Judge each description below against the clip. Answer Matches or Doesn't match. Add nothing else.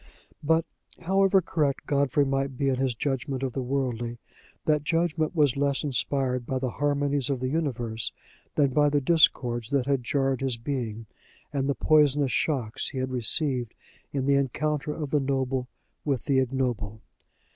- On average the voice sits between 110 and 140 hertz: Matches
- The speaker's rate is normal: Matches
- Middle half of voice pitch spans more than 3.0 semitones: Doesn't match